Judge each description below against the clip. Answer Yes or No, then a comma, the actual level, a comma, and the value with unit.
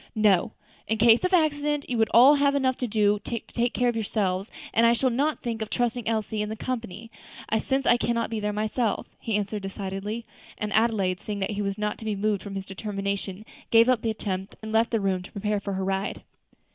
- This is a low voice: No, high, 220 Hz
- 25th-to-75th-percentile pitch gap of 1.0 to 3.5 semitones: Yes, average, 2.8 semitones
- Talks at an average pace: No, fast, 220 wpm